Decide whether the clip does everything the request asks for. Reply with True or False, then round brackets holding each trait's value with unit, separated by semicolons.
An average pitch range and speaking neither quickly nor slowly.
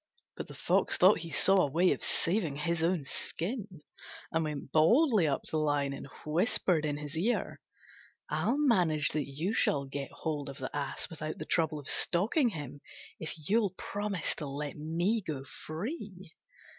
True (4.5 semitones; 175 wpm)